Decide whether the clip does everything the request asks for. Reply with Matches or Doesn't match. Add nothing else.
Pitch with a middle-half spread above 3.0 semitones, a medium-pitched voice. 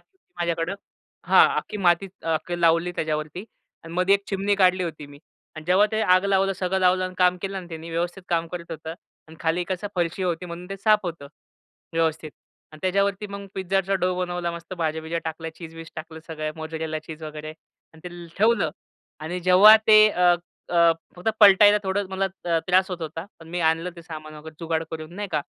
Doesn't match